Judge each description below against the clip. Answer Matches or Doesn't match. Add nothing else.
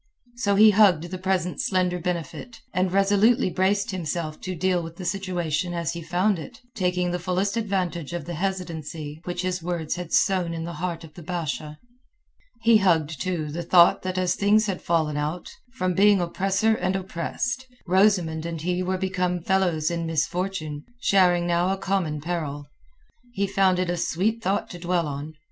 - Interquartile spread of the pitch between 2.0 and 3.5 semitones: Matches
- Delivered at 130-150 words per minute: Doesn't match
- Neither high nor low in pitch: Matches